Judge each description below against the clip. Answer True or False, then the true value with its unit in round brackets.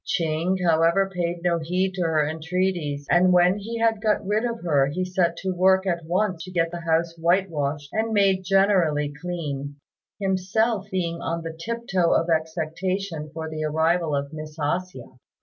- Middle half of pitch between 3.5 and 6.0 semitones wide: False (3.0 semitones)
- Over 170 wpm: True (180 wpm)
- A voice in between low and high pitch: True (175 Hz)